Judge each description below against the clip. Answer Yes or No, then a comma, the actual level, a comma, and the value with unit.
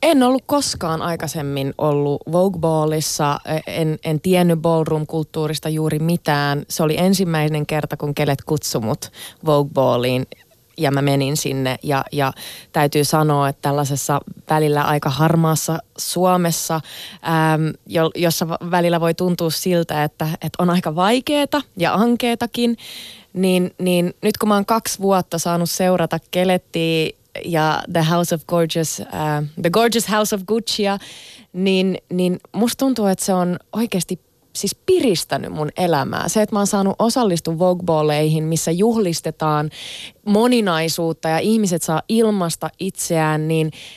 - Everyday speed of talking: Yes, average, 135 wpm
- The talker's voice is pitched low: No, medium, 165 Hz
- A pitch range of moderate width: Yes, average, 3.4 semitones